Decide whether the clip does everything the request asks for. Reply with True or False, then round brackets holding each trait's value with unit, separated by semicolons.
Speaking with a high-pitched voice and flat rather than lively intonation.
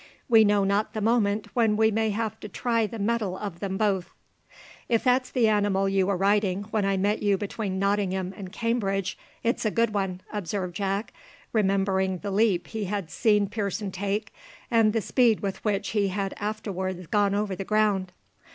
True (205 Hz; 2.0 semitones)